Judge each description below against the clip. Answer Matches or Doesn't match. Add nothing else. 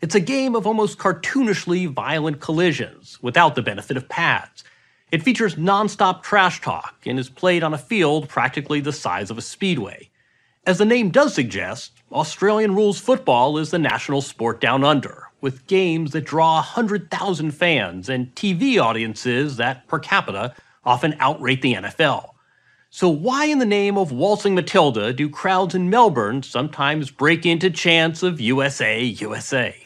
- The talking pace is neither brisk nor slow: Matches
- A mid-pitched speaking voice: Matches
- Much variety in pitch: Matches